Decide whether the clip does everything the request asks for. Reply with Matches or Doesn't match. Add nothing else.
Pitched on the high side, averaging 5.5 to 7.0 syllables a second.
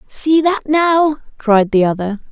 Doesn't match